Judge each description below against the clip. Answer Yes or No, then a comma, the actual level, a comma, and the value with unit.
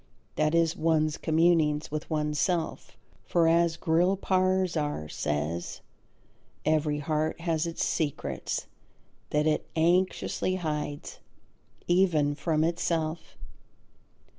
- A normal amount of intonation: No, narrow, 2.1 semitones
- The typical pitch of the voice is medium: Yes, medium, 160 Hz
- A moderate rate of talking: No, slow, 90 wpm